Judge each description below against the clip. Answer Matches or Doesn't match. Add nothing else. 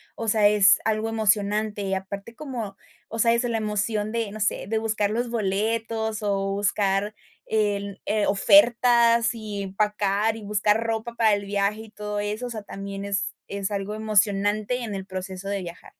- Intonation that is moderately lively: Doesn't match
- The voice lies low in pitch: Doesn't match